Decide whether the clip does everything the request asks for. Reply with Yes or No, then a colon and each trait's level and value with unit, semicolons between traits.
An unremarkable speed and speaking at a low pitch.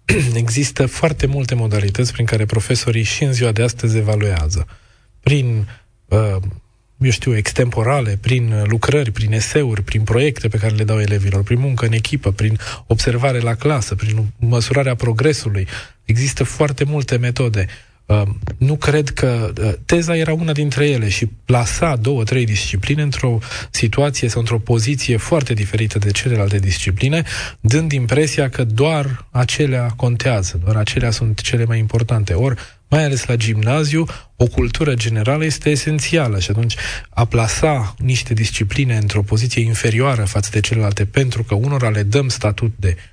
Yes: average, 150 wpm; low, 115 Hz